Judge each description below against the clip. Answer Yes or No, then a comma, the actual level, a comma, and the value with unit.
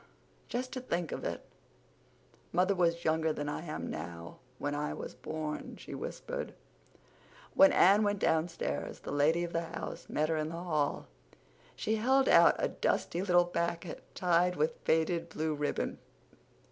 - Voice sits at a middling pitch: Yes, medium, 165 Hz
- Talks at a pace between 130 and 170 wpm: Yes, average, 155 wpm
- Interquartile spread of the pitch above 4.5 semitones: No, average, 2.7 semitones